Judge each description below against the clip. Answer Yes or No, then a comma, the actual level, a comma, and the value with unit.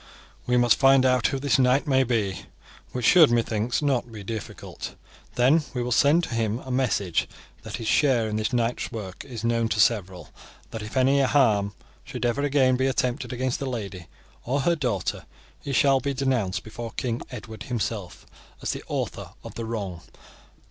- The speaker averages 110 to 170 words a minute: No, average, 185 wpm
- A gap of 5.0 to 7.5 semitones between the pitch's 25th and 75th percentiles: No, average, 3.4 semitones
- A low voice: Yes, low, 120 Hz